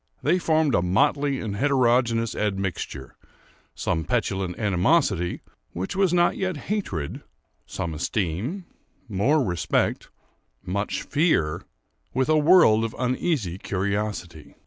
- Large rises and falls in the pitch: Yes, wide, 8.5 semitones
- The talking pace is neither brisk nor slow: No, slow, 105 wpm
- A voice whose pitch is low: Yes, low, 110 Hz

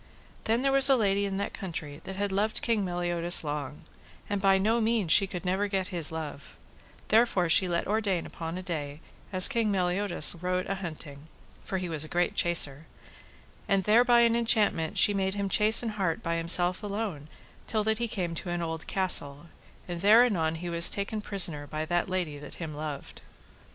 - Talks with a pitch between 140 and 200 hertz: Yes, medium, 185 Hz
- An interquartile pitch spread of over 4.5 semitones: No, average, 3.9 semitones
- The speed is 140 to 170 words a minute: No, average, 195 wpm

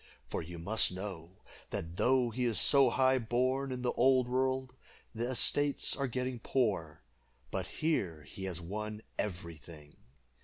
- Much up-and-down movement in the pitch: Yes, wide, 6.7 semitones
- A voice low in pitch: Yes, low, 115 Hz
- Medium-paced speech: Yes, average, 155 wpm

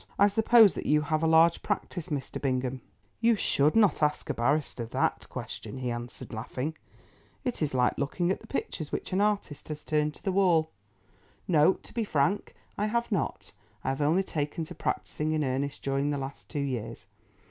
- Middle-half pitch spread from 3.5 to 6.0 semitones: Yes, average, 5.3 semitones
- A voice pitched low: No, medium, 150 Hz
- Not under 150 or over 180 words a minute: No, average, 190 wpm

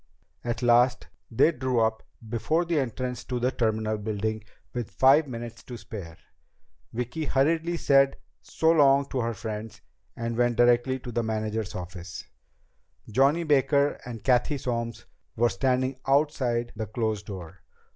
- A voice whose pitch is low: Yes, low, 120 Hz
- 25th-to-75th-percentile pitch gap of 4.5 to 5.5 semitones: No, average, 3.5 semitones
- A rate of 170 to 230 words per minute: No, average, 145 wpm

